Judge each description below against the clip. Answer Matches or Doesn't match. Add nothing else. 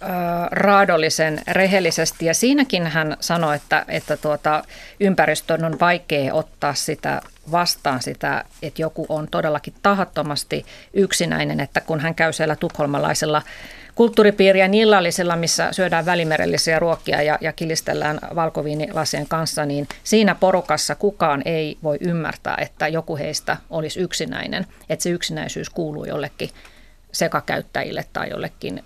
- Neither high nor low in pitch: Matches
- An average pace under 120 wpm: Doesn't match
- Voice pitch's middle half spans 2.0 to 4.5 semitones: Matches